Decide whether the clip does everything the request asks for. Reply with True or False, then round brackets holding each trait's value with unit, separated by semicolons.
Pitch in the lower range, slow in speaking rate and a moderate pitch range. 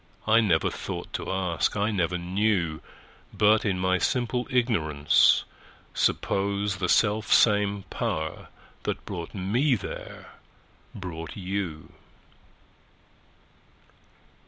True (100 Hz; 90 wpm; 3.4 semitones)